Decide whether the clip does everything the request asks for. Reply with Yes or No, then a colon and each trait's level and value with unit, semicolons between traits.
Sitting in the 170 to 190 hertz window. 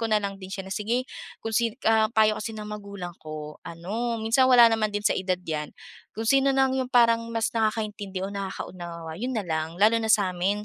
No: high, 210 Hz